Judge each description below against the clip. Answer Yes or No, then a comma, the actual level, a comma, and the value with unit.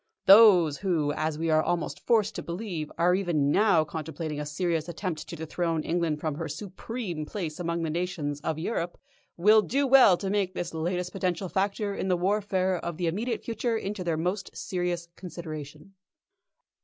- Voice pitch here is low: No, medium, 175 Hz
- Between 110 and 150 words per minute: No, average, 175 wpm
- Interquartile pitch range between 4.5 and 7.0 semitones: No, average, 3.5 semitones